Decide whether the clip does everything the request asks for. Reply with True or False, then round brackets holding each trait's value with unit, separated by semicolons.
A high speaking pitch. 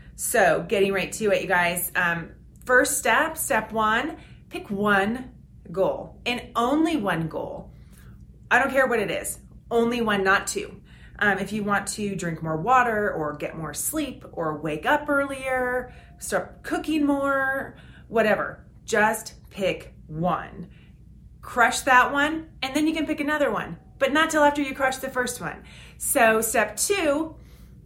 True (240 Hz)